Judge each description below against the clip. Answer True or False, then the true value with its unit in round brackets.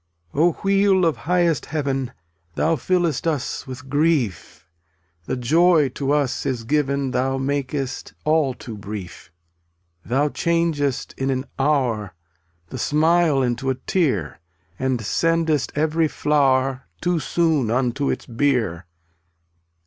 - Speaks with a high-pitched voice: False (140 Hz)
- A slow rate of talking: True (125 wpm)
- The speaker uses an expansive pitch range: False (3.9 semitones)